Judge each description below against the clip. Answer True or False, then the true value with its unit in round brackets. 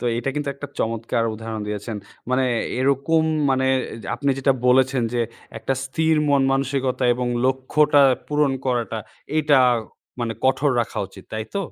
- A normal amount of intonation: True (3.1 semitones)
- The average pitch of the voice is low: True (130 Hz)